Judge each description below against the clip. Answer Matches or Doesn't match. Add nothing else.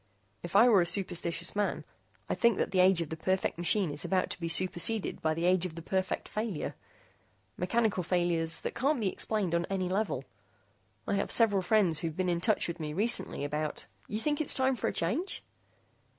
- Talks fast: Matches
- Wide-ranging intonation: Doesn't match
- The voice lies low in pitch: Doesn't match